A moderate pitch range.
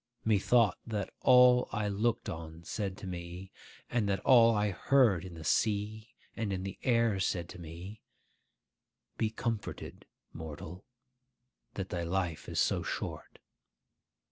Yes: average, 4.1 semitones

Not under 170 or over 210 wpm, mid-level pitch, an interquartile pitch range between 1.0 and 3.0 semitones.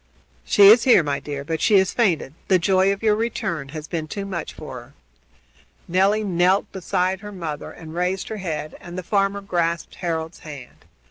No: average, 190 wpm; medium, 180 Hz; average, 3.8 semitones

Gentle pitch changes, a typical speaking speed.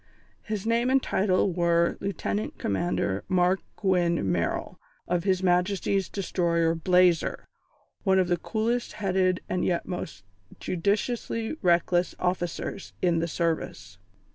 No: narrow, 2.3 semitones; slow, 120 wpm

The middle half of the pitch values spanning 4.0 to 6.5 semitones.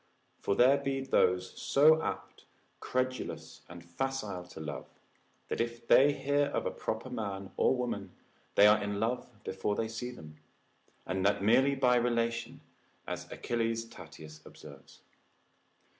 Yes: average, 5.1 semitones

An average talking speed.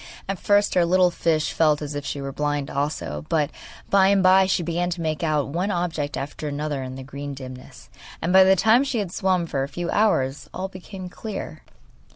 No: fast, 210 wpm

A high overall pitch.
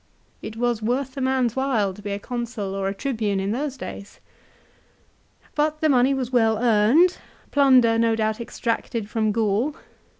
Yes: high, 235 Hz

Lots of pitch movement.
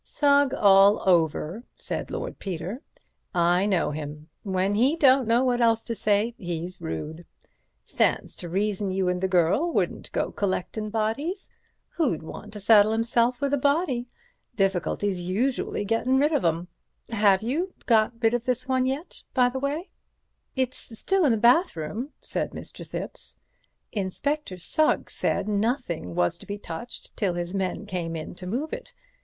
Yes: wide, 5.9 semitones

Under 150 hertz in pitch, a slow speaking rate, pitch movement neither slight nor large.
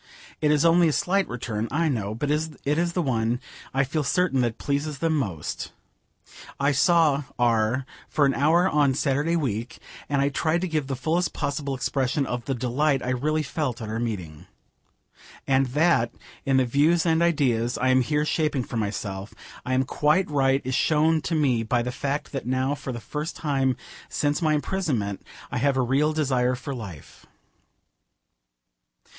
No: medium, 140 Hz; average, 180 wpm; average, 3.7 semitones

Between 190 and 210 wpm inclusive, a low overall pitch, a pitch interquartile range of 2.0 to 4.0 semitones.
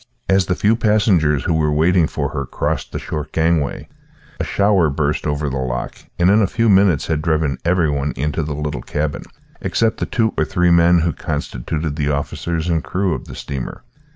Yes: average, 200 wpm; very low, 80 Hz; average, 3.6 semitones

